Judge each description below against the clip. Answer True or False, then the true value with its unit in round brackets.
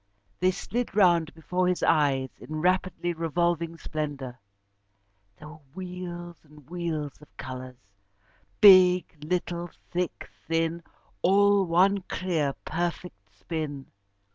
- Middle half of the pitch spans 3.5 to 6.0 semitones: False (3.1 semitones)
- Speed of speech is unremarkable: False (110 wpm)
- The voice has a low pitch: False (170 Hz)